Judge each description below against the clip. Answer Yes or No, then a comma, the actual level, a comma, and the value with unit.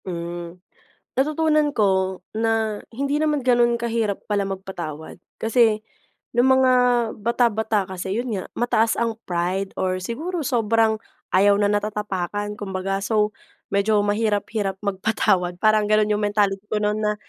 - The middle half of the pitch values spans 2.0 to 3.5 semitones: Yes, average, 2.9 semitones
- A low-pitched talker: No, high, 210 Hz